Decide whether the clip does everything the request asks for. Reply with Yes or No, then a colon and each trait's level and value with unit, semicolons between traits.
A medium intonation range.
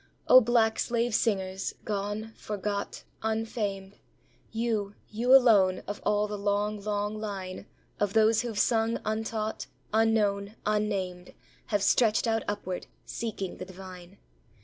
No: narrow, 1.9 semitones